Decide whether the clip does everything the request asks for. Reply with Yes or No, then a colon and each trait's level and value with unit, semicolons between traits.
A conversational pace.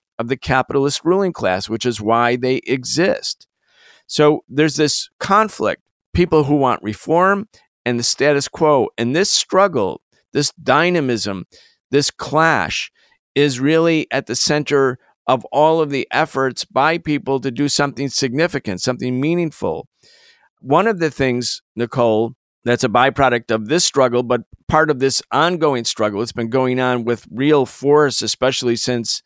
Yes: average, 150 wpm